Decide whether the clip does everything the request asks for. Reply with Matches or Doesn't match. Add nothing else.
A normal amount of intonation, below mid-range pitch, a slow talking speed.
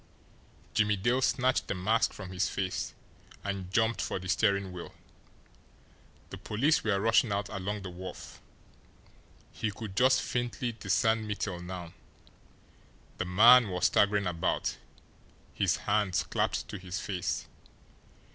Matches